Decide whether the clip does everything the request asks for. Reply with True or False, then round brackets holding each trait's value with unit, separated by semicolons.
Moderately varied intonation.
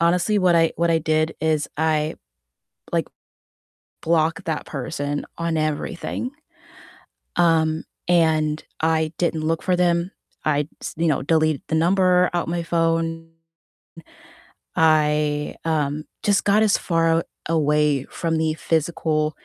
False (1.6 semitones)